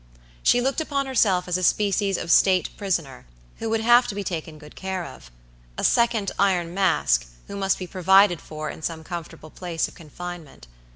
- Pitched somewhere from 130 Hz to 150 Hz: No, medium, 185 Hz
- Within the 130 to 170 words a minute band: No, average, 185 wpm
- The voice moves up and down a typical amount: Yes, average, 3.6 semitones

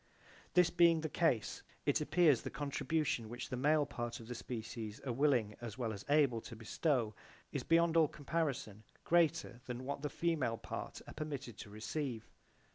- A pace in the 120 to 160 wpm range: No, average, 175 wpm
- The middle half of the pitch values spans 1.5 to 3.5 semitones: No, average, 5.1 semitones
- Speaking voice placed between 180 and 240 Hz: No, low, 135 Hz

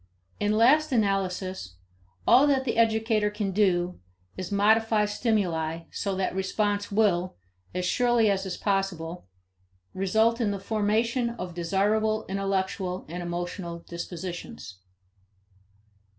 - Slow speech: Yes, slow, 115 wpm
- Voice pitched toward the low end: No, high, 195 Hz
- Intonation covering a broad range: No, average, 3.4 semitones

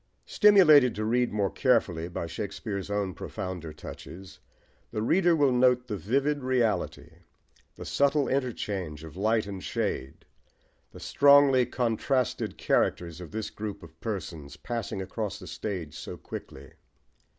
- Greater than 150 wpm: No, slow, 135 wpm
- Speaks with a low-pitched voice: Yes, low, 110 Hz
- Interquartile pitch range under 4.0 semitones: No, wide, 5.6 semitones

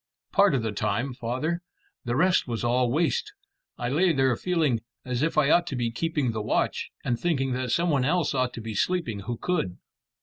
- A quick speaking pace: Yes, fast, 210 wpm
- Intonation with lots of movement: Yes, wide, 5.7 semitones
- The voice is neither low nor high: No, low, 130 Hz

